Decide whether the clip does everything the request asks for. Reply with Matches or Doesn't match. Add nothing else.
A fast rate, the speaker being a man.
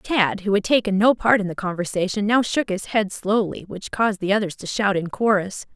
Doesn't match